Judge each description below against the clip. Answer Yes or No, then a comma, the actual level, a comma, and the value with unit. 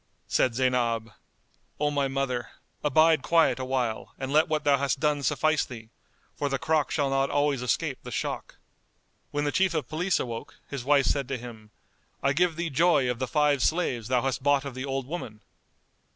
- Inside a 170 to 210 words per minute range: Yes, average, 190 wpm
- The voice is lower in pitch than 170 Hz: Yes, medium, 140 Hz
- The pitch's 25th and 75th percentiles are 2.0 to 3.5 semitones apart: Yes, average, 2.9 semitones